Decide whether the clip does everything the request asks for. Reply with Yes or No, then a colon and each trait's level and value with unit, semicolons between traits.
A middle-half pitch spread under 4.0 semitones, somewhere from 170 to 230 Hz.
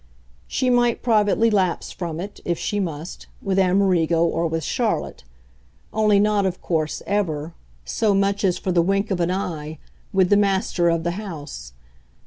Yes: average, 3.4 semitones; medium, 185 Hz